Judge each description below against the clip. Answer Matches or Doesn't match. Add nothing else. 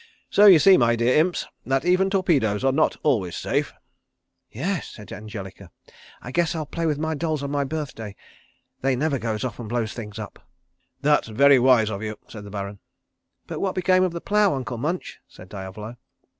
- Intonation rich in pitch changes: Matches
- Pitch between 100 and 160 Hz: Matches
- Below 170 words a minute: Doesn't match